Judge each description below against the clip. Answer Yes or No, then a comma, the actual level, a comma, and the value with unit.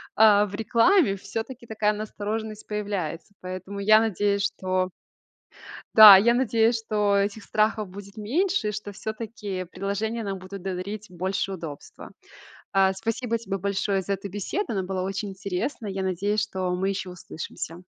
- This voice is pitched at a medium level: No, high, 200 Hz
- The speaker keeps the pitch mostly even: Yes, narrow, 2.2 semitones